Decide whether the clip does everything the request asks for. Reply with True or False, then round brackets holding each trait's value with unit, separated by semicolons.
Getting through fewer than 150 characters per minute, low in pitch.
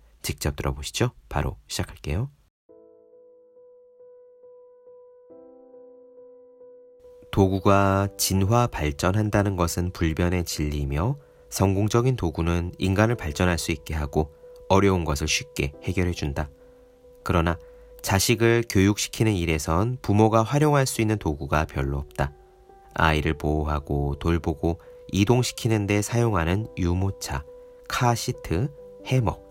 False (245 characters per minute; 105 Hz)